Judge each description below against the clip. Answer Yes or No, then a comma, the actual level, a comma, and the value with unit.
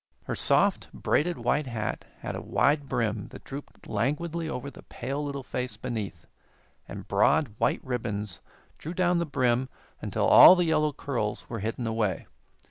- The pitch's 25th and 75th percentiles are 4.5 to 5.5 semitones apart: Yes, average, 5.0 semitones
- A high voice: No, low, 130 Hz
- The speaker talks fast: No, average, 160 wpm